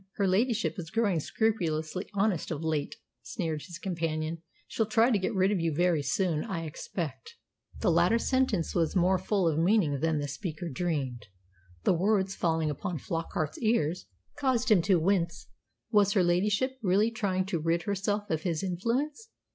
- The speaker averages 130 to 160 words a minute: No, average, 170 wpm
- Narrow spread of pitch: No, average, 4.4 semitones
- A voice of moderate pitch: Yes, medium, 180 Hz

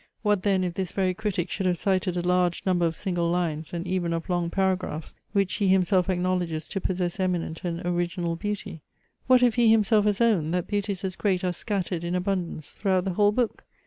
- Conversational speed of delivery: No, fast, 210 wpm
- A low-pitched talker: No, medium, 185 Hz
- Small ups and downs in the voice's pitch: Yes, narrow, 2.3 semitones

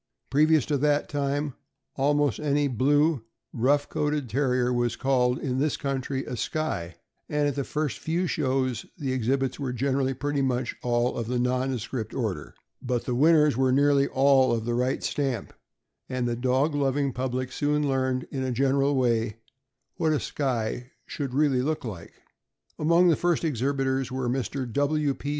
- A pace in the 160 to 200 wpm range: Yes, average, 165 wpm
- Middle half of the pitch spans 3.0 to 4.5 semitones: No, narrow, 2.6 semitones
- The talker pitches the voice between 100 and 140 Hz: Yes, low, 135 Hz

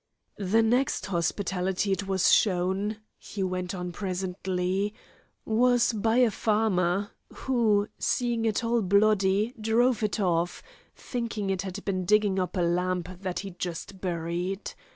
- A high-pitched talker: Yes, high, 195 Hz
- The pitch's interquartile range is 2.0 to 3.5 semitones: Yes, average, 3.0 semitones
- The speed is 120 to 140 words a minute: Yes, slow, 135 wpm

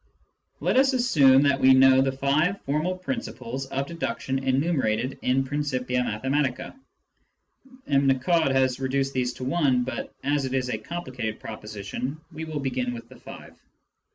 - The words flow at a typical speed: Yes, average, 155 wpm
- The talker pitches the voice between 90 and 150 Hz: Yes, low, 135 Hz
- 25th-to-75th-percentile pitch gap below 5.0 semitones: Yes, narrow, 2.5 semitones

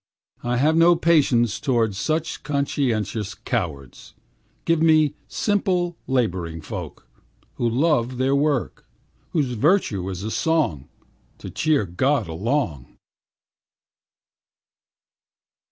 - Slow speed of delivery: Yes, slow, 95 wpm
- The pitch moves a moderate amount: No, wide, 7.0 semitones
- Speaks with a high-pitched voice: No, low, 130 Hz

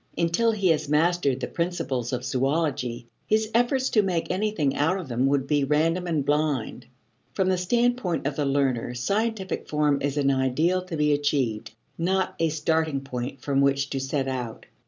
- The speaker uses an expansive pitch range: No, average, 4.8 semitones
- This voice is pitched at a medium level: Yes, medium, 150 Hz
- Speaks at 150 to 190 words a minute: Yes, average, 175 wpm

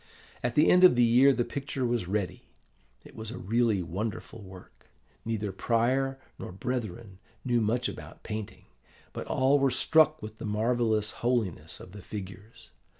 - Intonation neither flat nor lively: Yes, average, 3.3 semitones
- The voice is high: No, low, 115 Hz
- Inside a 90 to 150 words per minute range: No, average, 160 wpm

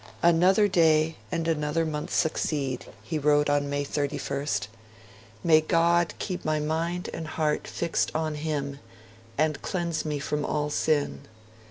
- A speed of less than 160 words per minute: Yes, average, 140 wpm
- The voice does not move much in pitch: Yes, narrow, 2.0 semitones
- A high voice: No, medium, 155 Hz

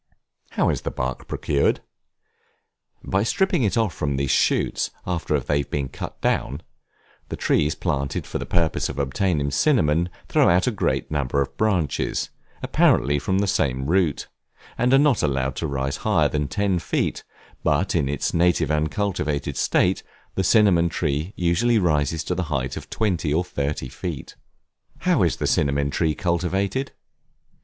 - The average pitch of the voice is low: Yes, very low, 80 Hz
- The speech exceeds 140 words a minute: Yes, average, 160 wpm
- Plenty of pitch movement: No, average, 5.0 semitones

